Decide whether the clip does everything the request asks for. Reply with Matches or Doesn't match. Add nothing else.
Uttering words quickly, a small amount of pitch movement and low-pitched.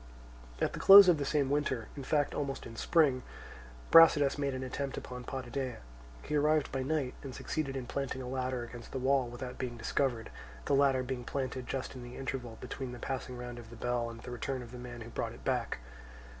Matches